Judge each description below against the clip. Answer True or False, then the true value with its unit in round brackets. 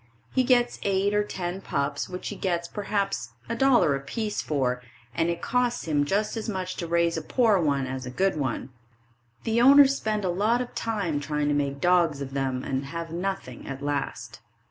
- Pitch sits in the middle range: True (175 Hz)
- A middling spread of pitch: False (6.7 semitones)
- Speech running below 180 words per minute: False (190 wpm)